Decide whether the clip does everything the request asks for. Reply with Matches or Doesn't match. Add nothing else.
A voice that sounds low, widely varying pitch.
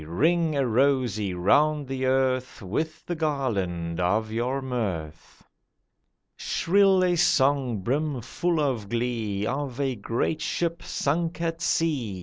Matches